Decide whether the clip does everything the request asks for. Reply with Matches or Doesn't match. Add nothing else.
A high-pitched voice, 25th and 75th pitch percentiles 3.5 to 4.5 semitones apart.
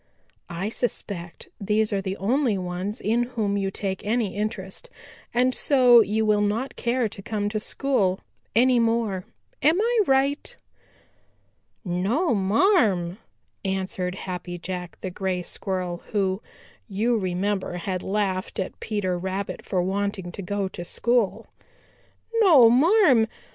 Matches